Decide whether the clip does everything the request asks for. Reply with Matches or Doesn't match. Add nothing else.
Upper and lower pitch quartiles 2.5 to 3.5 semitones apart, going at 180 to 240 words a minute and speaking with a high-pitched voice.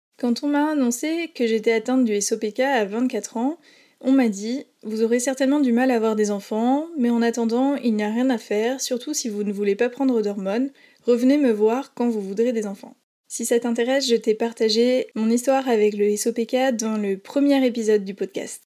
Matches